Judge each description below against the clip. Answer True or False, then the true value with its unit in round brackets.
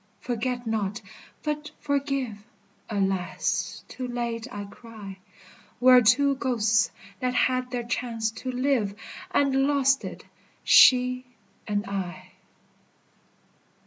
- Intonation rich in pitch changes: False (3.3 semitones)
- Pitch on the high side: True (245 Hz)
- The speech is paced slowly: True (110 wpm)